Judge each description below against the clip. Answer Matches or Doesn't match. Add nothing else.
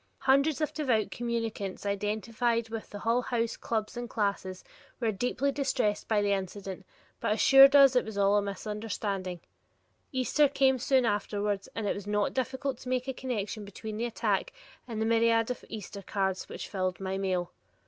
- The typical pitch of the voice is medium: Doesn't match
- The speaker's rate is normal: Matches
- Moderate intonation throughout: Matches